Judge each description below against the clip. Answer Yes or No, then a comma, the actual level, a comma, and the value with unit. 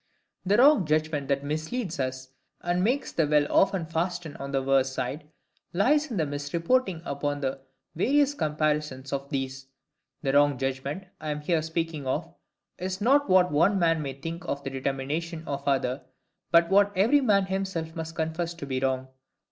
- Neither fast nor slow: Yes, average, 170 wpm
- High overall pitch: No, medium, 155 Hz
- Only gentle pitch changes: No, average, 4.6 semitones